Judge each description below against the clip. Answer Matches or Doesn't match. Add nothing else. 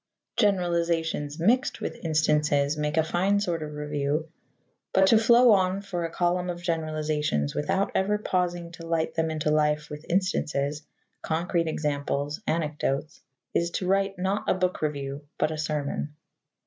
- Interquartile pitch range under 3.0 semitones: Doesn't match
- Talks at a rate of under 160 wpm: Matches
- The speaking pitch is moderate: Matches